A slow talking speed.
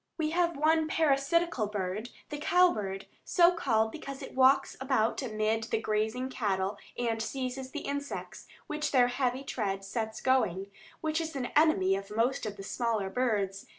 No: average, 165 wpm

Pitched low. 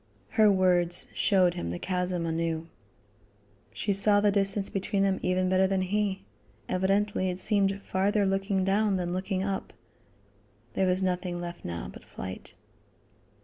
No: high, 190 Hz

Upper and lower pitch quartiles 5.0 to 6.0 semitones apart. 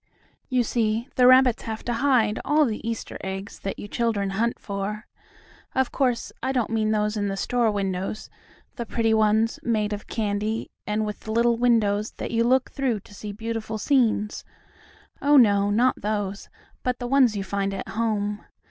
No: narrow, 2.5 semitones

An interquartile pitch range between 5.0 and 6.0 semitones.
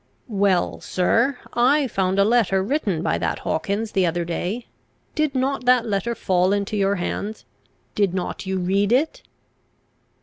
No: average, 4.5 semitones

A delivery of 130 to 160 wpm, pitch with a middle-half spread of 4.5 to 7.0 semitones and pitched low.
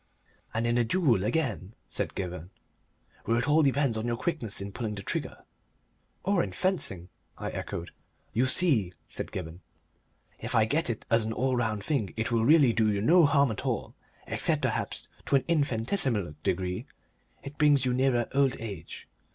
No: average, 175 wpm; average, 5.0 semitones; low, 120 Hz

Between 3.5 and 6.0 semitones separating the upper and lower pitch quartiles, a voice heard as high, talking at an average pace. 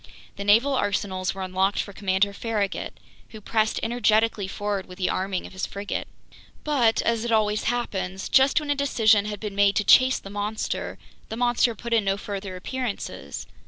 No: average, 2.9 semitones; high, 210 Hz; average, 180 wpm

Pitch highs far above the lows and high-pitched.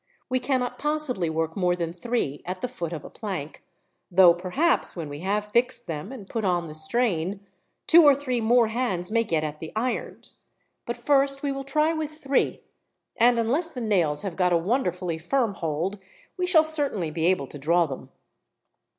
Yes: wide, 7.2 semitones; high, 210 Hz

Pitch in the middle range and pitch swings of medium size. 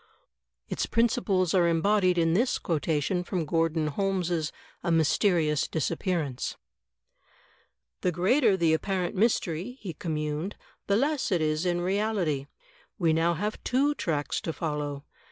Yes: medium, 175 Hz; average, 3.8 semitones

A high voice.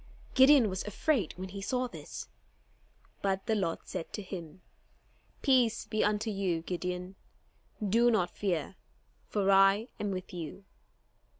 Yes: high, 195 Hz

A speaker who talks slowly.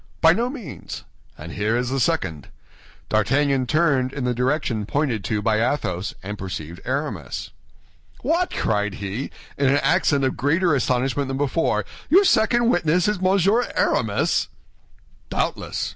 No: average, 145 wpm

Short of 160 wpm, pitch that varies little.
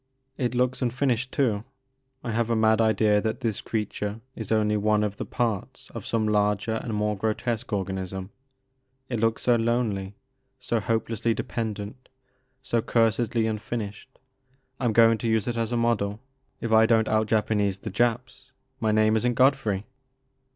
No: average, 165 wpm; narrow, 2.0 semitones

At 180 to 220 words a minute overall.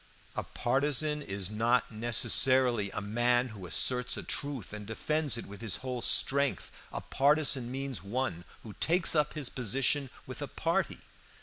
No: average, 160 wpm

